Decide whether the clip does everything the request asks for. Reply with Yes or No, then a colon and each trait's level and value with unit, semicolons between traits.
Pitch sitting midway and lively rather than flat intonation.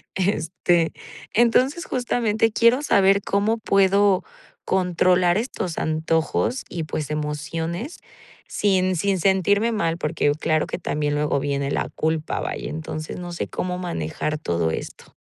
No: medium, 180 Hz; average, 4.5 semitones